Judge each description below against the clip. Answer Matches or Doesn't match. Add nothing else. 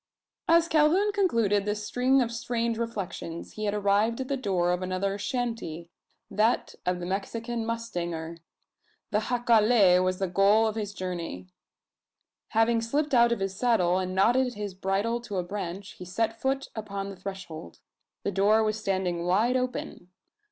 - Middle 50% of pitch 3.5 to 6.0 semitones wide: Matches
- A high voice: Matches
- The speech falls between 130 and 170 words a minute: Matches